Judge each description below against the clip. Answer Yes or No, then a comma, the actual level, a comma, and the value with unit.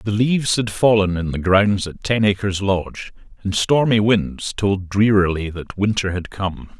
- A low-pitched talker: Yes, low, 100 Hz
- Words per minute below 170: No, average, 175 wpm